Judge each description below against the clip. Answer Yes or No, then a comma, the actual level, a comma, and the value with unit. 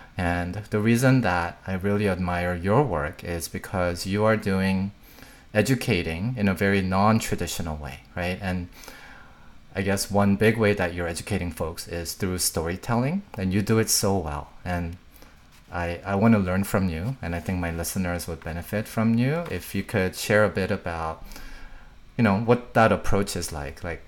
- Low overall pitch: Yes, very low, 95 Hz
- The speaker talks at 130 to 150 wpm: No, average, 180 wpm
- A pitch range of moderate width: Yes, average, 3.4 semitones